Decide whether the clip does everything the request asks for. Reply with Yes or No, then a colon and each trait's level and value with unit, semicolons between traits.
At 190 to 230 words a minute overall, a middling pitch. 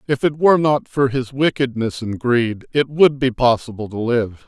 No: average, 200 wpm; low, 125 Hz